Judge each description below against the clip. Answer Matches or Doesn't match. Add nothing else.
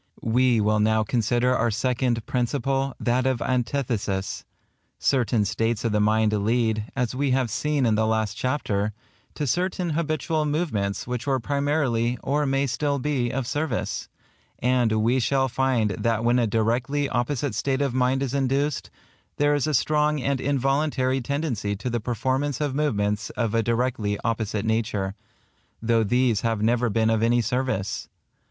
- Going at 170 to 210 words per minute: Doesn't match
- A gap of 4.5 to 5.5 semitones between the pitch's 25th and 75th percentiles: Doesn't match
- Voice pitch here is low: Matches